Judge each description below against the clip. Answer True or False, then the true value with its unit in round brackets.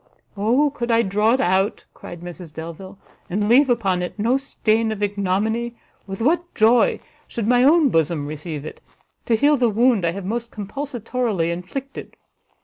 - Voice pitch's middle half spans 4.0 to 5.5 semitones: True (4.7 semitones)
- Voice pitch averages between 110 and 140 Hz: False (220 Hz)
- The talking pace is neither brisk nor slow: True (165 wpm)